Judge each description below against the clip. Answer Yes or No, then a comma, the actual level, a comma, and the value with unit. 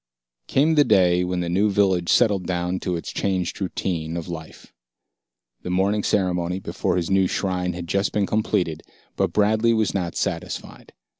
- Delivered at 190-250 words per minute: No, average, 165 wpm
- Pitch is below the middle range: Yes, very low, 95 Hz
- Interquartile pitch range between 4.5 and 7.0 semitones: No, narrow, 2.5 semitones